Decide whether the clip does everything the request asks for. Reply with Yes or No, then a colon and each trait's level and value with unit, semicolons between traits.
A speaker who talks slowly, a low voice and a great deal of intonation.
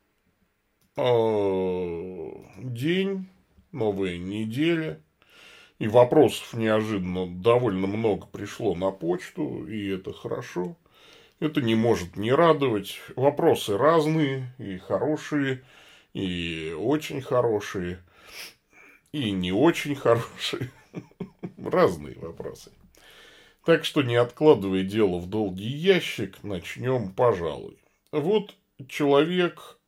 Yes: slow, 90 wpm; low, 115 Hz; wide, 7.8 semitones